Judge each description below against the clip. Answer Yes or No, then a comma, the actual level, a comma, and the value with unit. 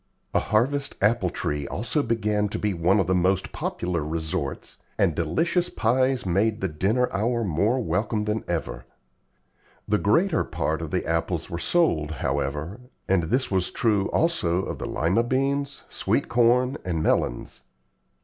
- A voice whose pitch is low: Yes, low, 100 Hz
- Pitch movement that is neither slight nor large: No, wide, 6.2 semitones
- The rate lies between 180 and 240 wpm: No, average, 155 wpm